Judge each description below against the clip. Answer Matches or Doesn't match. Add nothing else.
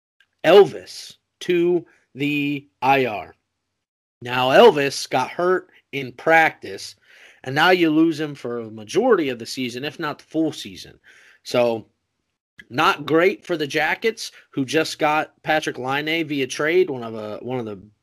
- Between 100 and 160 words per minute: Matches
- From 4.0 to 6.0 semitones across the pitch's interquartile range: Matches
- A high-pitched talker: Doesn't match